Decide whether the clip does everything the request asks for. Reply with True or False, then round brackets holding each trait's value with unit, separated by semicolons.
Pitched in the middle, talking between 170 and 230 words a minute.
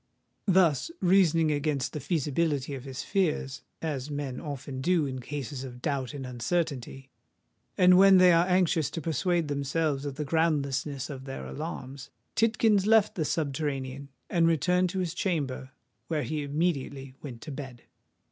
False (145 Hz; 145 wpm)